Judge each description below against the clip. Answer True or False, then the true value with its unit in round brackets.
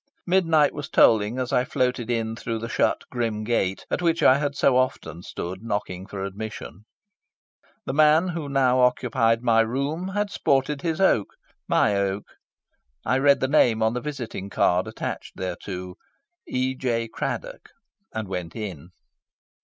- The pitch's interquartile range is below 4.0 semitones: False (5.2 semitones)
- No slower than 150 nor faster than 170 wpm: True (155 wpm)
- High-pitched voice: False (120 Hz)